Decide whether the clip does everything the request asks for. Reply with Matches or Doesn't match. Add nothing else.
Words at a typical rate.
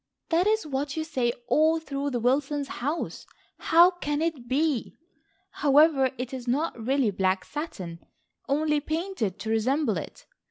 Matches